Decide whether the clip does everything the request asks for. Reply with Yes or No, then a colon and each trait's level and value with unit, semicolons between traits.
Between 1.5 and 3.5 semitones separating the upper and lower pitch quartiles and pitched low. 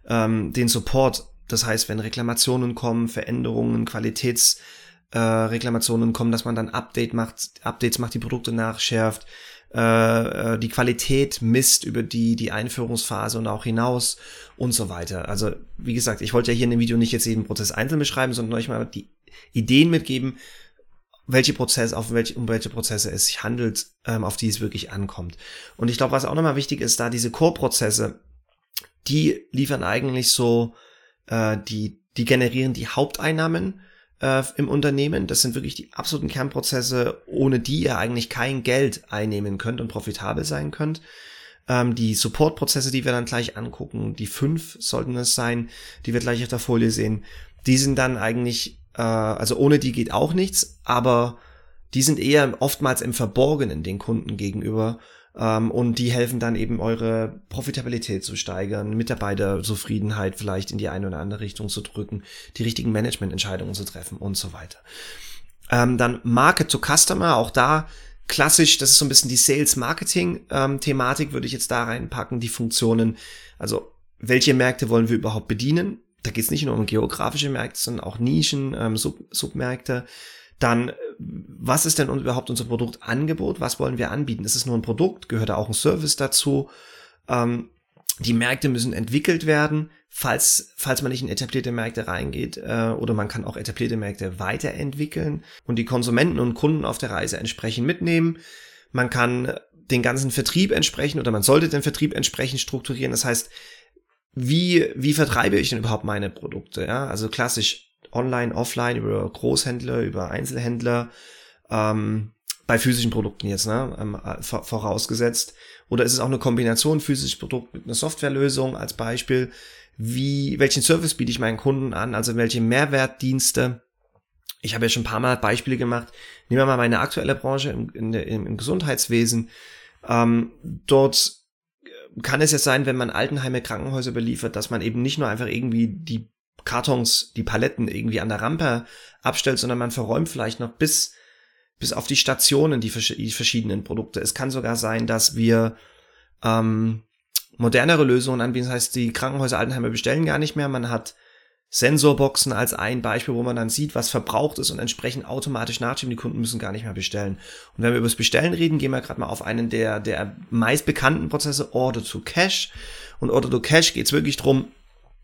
Yes: average, 3.1 semitones; low, 120 Hz